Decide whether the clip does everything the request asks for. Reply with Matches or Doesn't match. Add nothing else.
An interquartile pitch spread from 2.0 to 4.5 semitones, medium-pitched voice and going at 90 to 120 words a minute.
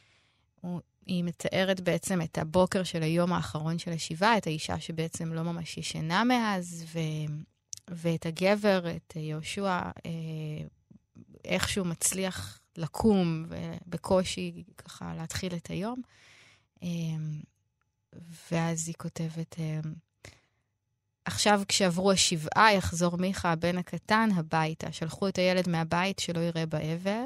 Matches